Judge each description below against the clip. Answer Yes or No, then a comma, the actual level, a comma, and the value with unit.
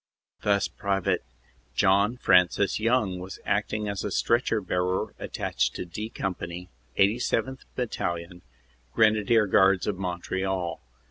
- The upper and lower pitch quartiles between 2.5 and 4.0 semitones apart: Yes, average, 2.9 semitones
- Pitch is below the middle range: Yes, low, 100 Hz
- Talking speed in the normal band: No, slow, 115 wpm